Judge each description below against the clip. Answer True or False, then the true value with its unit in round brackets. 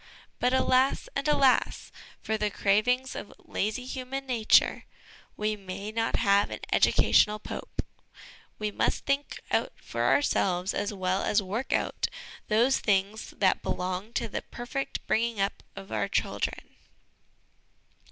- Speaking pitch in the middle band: False (215 Hz)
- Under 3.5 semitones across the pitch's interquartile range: False (4.2 semitones)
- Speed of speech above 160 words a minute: False (135 wpm)